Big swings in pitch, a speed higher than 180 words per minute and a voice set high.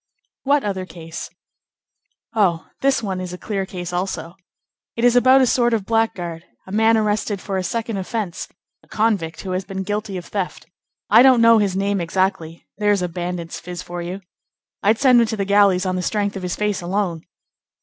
No: average, 3.5 semitones; average, 195 wpm; high, 195 Hz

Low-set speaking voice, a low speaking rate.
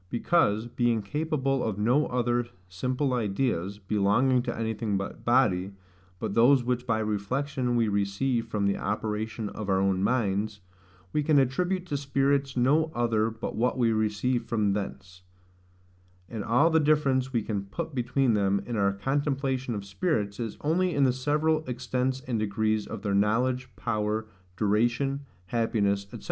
No: low, 120 Hz; average, 155 wpm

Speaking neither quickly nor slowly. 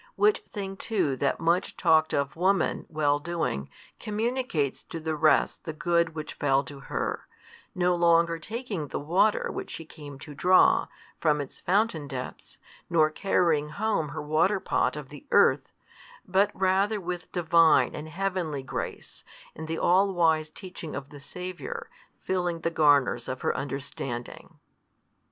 Yes: average, 150 wpm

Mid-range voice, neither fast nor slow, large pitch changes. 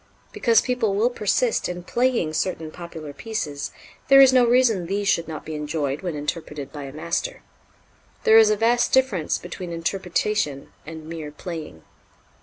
Yes: medium, 175 Hz; average, 160 wpm; wide, 6.4 semitones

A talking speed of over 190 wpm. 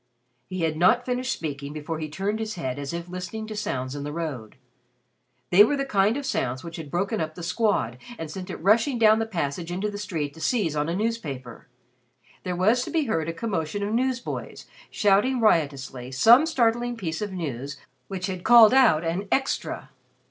Yes: average, 200 wpm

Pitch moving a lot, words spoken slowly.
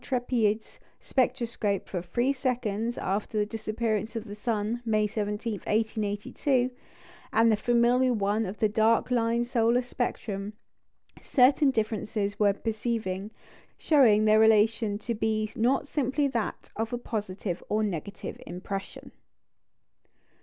No: narrow, 2.5 semitones; slow, 125 wpm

